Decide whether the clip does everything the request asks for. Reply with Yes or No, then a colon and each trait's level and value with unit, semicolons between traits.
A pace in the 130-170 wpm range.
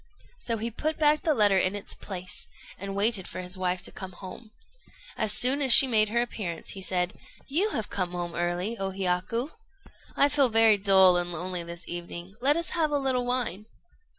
No: average, 200 wpm